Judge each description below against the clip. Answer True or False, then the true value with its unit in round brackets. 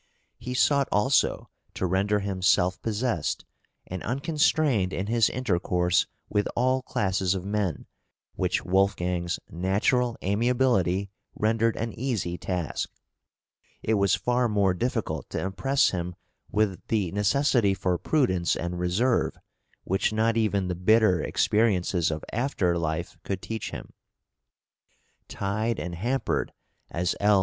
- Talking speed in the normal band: False (125 wpm)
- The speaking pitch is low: True (100 Hz)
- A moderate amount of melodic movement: True (4.4 semitones)